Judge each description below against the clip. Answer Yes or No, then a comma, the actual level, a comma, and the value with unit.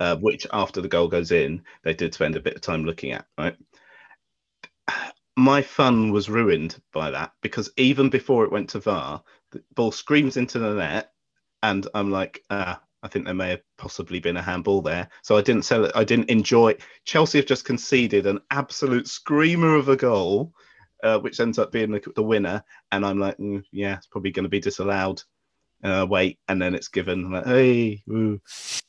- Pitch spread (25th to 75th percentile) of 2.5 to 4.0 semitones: No, average, 4.8 semitones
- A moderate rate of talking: No, fast, 210 wpm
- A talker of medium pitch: No, low, 105 Hz